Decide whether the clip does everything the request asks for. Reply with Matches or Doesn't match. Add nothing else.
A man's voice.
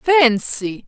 Doesn't match